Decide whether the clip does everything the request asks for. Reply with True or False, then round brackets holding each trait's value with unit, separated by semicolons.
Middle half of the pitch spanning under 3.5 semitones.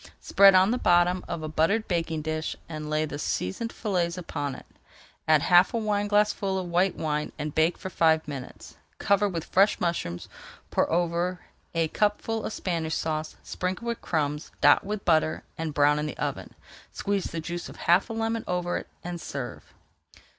False (3.8 semitones)